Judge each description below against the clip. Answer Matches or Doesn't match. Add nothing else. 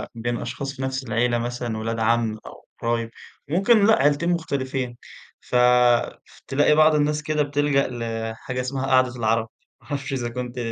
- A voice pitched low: Matches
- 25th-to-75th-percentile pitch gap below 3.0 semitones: Doesn't match